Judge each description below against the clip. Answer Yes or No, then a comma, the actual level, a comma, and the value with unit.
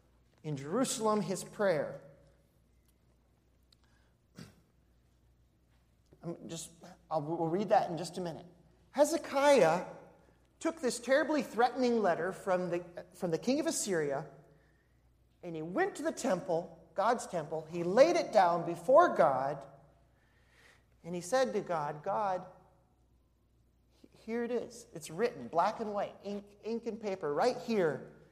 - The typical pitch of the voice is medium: Yes, medium, 180 Hz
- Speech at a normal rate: No, slow, 130 wpm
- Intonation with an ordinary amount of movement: No, wide, 7.1 semitones